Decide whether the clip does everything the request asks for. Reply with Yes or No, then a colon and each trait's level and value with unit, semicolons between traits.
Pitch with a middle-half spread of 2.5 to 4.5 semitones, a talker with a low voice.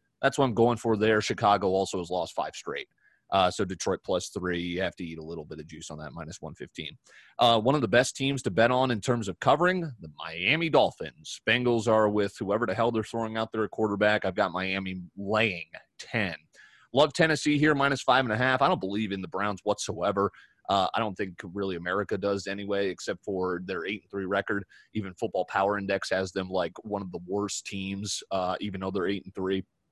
Yes: average, 3.4 semitones; low, 100 Hz